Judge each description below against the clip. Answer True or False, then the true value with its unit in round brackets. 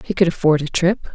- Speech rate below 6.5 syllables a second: True (5.8 syllables/s)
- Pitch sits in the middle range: True (170 Hz)